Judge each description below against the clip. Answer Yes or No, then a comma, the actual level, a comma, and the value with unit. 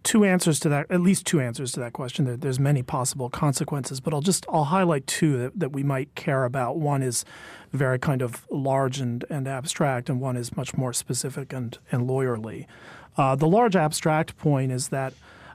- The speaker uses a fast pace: No, average, 195 wpm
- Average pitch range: Yes, average, 3.5 semitones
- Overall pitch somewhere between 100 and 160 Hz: Yes, medium, 140 Hz